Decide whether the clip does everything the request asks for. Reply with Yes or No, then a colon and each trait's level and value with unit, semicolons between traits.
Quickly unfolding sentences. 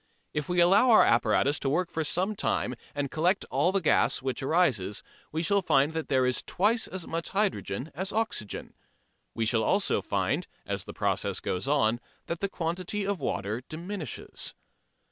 No: average, 175 wpm